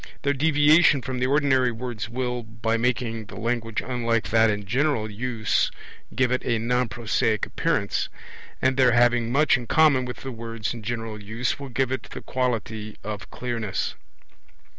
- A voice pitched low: Yes, low, 120 Hz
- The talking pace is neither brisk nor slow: Yes, average, 165 wpm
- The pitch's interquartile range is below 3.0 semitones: Yes, narrow, 2.4 semitones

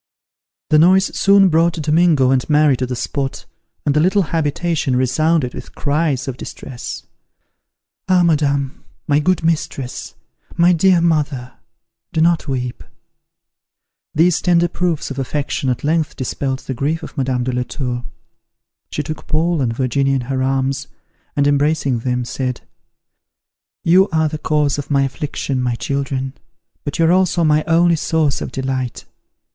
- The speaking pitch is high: No, medium, 145 Hz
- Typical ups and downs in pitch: Yes, average, 3.6 semitones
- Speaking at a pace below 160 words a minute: Yes, average, 150 wpm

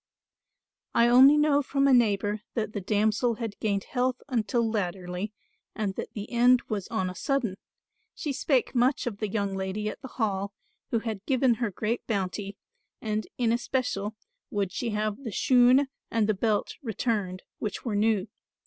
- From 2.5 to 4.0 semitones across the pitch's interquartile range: Yes, average, 3.3 semitones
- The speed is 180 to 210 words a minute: No, average, 170 wpm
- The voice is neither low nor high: No, high, 220 Hz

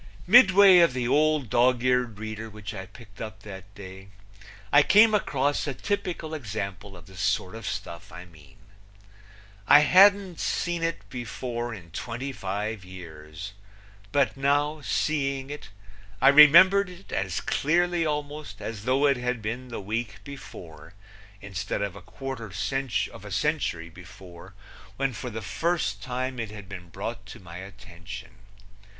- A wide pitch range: Yes, wide, 6.8 semitones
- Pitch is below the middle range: Yes, low, 115 Hz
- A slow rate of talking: No, average, 150 wpm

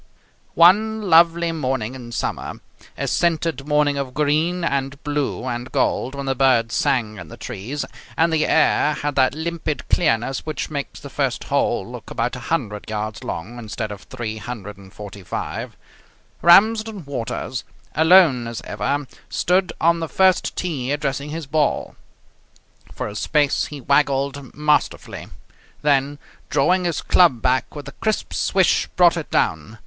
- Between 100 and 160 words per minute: Yes, average, 145 wpm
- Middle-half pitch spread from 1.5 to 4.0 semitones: No, average, 5.1 semitones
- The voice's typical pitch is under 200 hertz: Yes, medium, 140 Hz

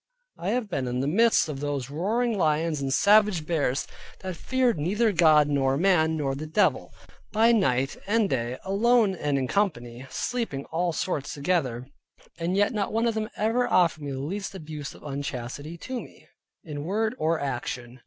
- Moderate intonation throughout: No, wide, 6.7 semitones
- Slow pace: No, average, 180 wpm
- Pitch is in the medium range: Yes, medium, 160 Hz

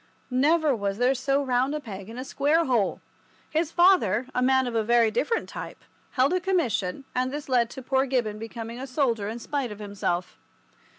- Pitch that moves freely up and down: No, average, 4.0 semitones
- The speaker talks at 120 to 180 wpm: No, average, 195 wpm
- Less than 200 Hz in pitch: No, very high, 255 Hz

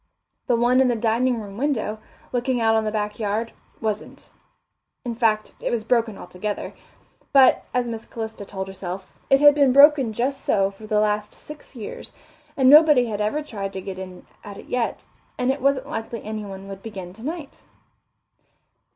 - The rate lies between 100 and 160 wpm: No, average, 175 wpm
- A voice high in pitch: Yes, high, 225 Hz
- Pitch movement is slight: No, average, 3.7 semitones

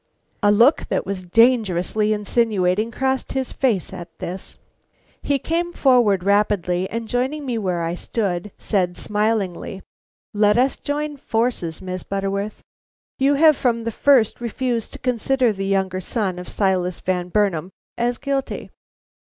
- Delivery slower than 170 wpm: Yes, average, 145 wpm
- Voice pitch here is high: Yes, high, 210 Hz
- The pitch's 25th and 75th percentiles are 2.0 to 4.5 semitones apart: No, average, 4.9 semitones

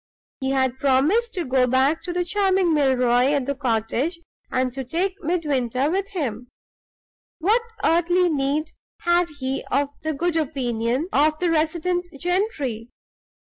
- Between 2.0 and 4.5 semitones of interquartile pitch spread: No, average, 5.2 semitones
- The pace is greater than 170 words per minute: No, average, 140 wpm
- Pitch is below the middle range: No, very high, 300 Hz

